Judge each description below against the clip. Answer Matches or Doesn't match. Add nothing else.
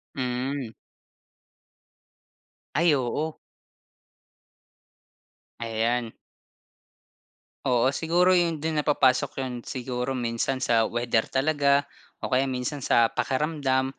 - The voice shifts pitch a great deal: Doesn't match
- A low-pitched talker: Matches